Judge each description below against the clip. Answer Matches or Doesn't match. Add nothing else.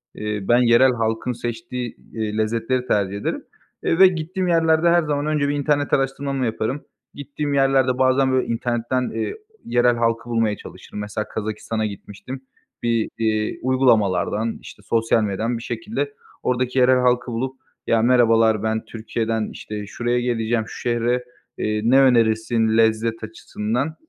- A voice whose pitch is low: Matches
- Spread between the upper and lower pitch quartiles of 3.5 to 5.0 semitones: Doesn't match